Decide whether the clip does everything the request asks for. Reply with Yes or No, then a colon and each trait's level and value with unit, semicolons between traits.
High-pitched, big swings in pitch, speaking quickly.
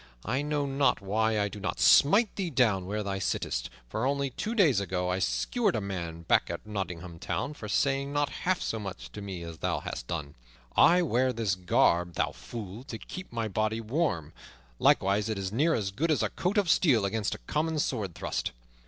No: low, 110 Hz; wide, 6.8 semitones; fast, 210 wpm